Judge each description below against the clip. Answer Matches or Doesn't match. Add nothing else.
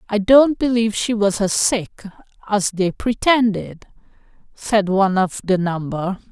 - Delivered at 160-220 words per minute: Doesn't match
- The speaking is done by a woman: Matches